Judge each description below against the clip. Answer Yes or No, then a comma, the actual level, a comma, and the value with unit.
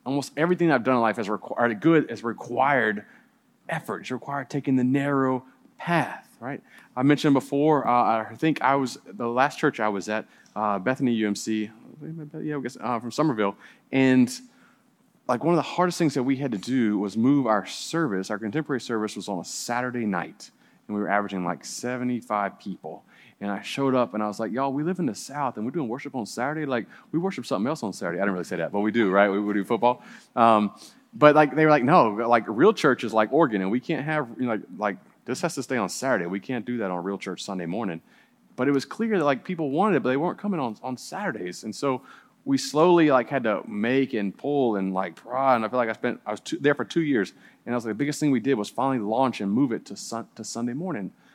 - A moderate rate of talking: No, fast, 245 wpm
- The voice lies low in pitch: Yes, low, 125 Hz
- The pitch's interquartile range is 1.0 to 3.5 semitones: No, average, 5.3 semitones